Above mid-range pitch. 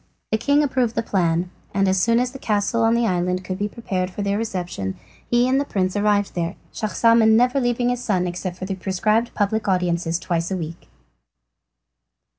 Yes: high, 205 Hz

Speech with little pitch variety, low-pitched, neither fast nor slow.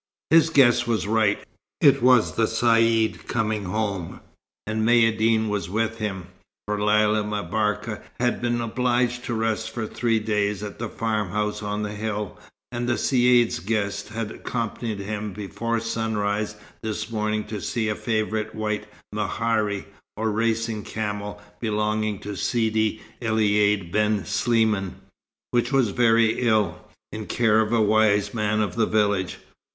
Yes: narrow, 1.6 semitones; low, 110 Hz; average, 145 wpm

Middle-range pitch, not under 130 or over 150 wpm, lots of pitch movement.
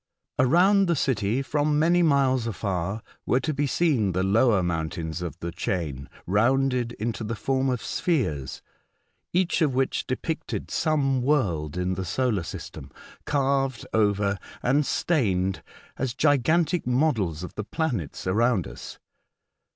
No: low, 120 Hz; slow, 135 wpm; wide, 7.2 semitones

